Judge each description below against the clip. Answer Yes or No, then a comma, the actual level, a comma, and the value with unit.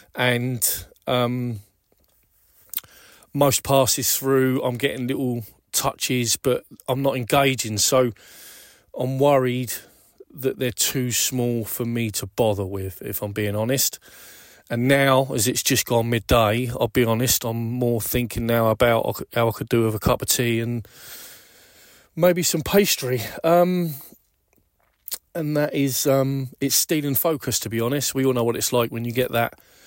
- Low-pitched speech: Yes, low, 125 Hz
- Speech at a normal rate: Yes, average, 155 wpm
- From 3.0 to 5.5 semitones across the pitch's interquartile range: No, narrow, 2.6 semitones